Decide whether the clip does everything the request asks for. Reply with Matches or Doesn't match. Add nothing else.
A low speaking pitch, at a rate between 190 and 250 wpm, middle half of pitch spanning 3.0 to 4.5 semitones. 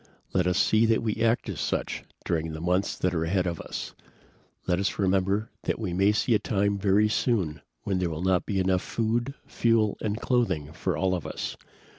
Matches